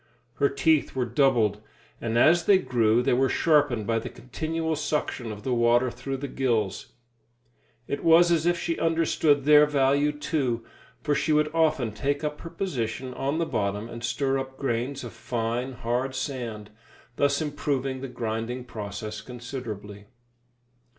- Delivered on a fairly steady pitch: No, average, 4.2 semitones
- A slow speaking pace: No, average, 155 wpm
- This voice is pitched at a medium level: No, low, 130 Hz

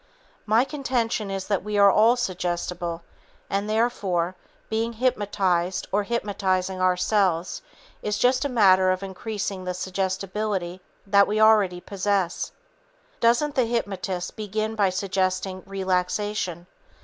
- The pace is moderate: No, slow, 120 wpm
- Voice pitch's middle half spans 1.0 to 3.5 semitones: Yes, average, 2.7 semitones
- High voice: Yes, high, 195 Hz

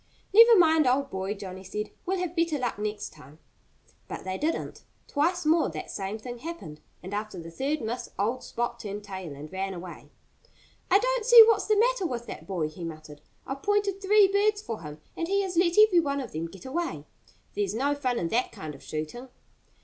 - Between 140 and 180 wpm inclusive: No, fast, 205 wpm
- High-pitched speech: Yes, very high, 250 Hz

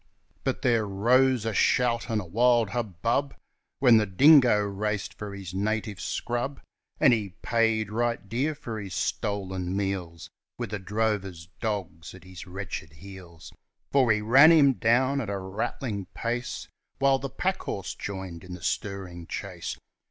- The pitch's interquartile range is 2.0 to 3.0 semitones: No, average, 4.0 semitones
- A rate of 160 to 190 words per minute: No, average, 150 wpm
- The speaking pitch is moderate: No, low, 105 Hz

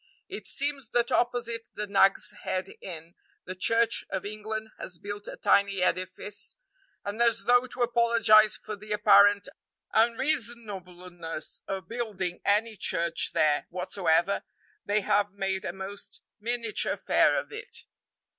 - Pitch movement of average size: Yes, average, 3.5 semitones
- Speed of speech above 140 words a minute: No, slow, 135 wpm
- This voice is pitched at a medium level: No, high, 205 Hz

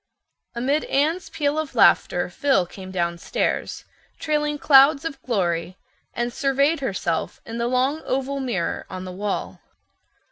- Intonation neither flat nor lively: No, wide, 7.1 semitones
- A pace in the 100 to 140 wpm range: Yes, slow, 135 wpm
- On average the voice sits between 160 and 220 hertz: No, very high, 260 Hz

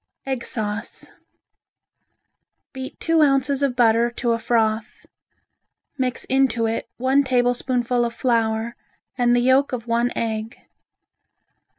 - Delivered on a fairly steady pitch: Yes, narrow, 2.3 semitones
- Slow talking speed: Yes, slow, 115 wpm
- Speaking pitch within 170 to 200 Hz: No, high, 245 Hz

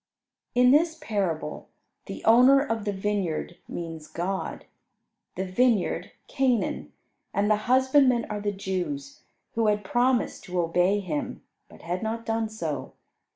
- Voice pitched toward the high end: Yes, high, 210 Hz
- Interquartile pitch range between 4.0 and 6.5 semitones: Yes, average, 5.3 semitones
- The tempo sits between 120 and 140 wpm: Yes, slow, 135 wpm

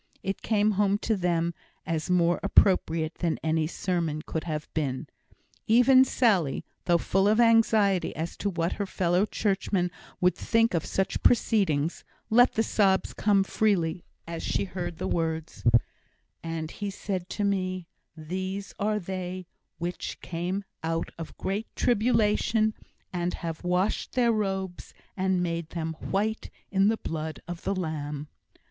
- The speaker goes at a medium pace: Yes, average, 145 wpm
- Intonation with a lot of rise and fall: No, average, 3.6 semitones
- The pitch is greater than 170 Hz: Yes, medium, 185 Hz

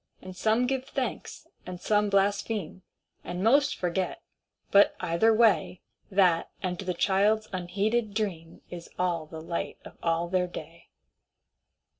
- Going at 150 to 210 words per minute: No, slow, 135 wpm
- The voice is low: No, high, 190 Hz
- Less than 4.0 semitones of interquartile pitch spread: Yes, average, 3.6 semitones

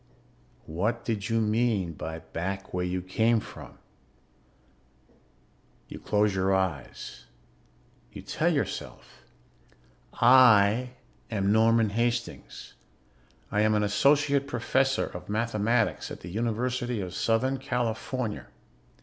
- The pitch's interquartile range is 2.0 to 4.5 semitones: Yes, average, 3.6 semitones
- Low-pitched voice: Yes, low, 110 Hz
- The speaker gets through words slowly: Yes, slow, 105 wpm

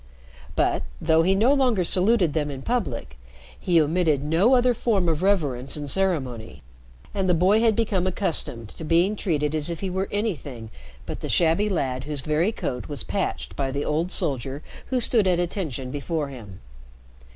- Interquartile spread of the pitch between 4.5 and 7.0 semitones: Yes, wide, 5.5 semitones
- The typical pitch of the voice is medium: Yes, medium, 165 Hz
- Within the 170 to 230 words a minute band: Yes, average, 175 wpm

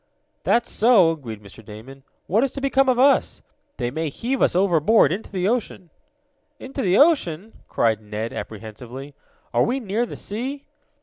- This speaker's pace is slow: No, average, 165 wpm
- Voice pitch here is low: No, medium, 185 Hz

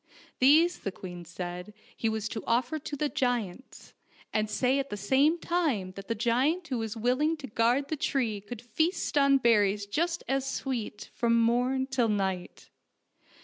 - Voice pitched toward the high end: Yes, high, 245 Hz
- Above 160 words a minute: Yes, average, 170 wpm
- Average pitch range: Yes, average, 4.7 semitones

